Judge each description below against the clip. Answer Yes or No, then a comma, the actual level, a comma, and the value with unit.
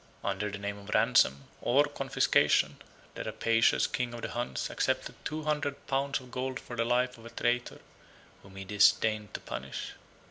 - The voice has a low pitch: Yes, low, 120 Hz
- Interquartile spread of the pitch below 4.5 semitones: Yes, average, 4.0 semitones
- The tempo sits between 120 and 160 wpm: No, average, 175 wpm